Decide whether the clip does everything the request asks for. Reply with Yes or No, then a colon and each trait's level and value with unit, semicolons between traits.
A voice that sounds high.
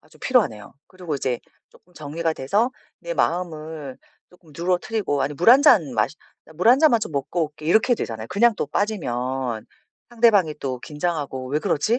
No: medium, 160 Hz